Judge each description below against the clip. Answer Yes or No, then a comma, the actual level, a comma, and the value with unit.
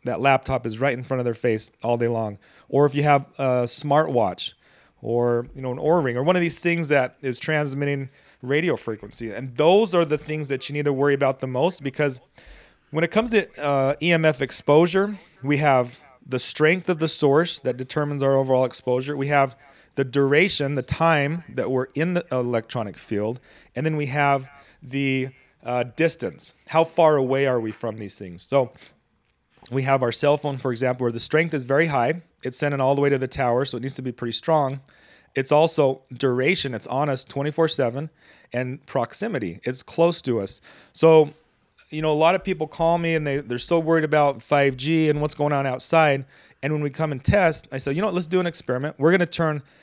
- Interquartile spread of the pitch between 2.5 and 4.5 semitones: Yes, average, 3.5 semitones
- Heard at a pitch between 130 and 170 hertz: Yes, medium, 140 Hz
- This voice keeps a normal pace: No, fast, 210 wpm